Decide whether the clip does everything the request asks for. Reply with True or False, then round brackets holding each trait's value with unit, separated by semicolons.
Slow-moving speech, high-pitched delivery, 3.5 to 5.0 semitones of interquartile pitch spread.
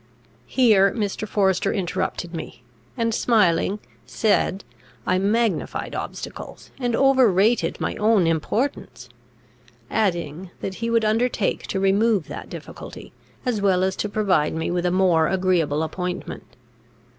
True (130 wpm; 195 Hz; 3.8 semitones)